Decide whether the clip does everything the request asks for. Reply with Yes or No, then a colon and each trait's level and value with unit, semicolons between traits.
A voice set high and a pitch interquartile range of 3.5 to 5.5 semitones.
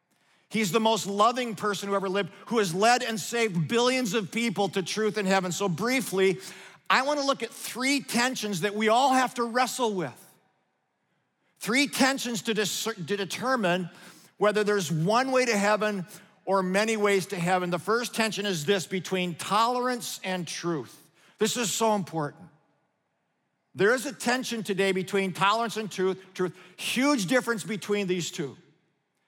Yes: high, 210 Hz; average, 3.8 semitones